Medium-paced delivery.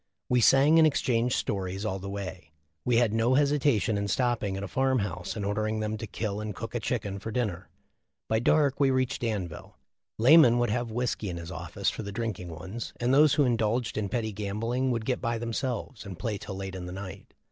No: fast, 220 wpm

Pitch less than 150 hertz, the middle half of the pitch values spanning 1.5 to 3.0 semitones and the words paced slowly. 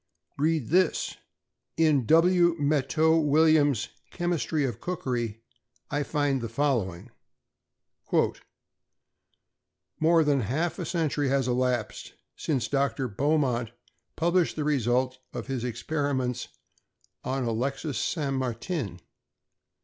No: medium, 140 Hz; average, 4.2 semitones; slow, 100 wpm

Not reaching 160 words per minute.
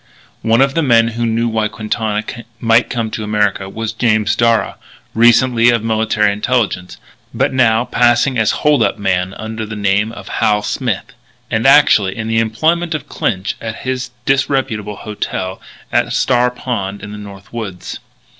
No: average, 170 wpm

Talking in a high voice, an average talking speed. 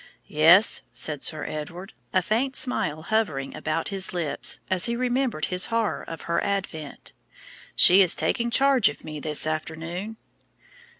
No: medium, 180 Hz; average, 145 wpm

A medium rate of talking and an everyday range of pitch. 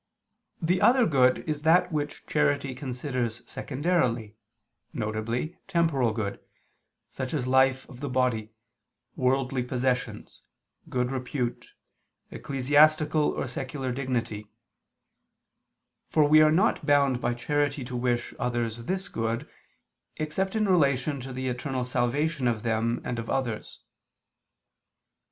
No: slow, 120 wpm; average, 3.5 semitones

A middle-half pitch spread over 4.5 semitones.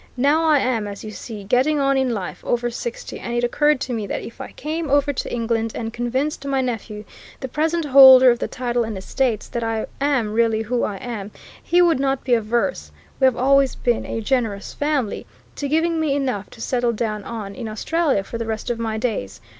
No: average, 3.7 semitones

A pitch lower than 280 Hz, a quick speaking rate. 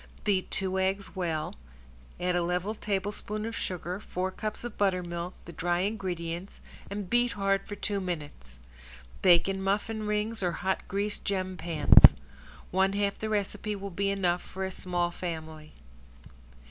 No: high, 190 Hz; average, 155 wpm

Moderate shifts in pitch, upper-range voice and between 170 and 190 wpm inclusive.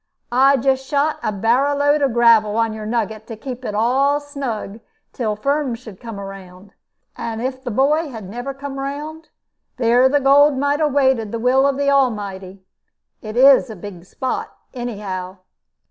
Yes: average, 4.4 semitones; very high, 250 Hz; average, 175 wpm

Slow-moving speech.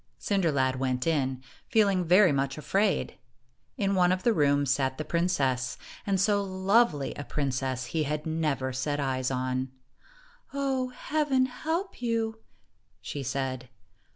No: average, 150 wpm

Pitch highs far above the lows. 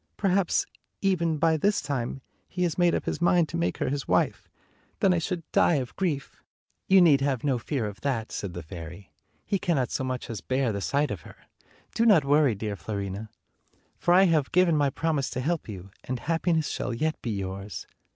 Yes: wide, 7.3 semitones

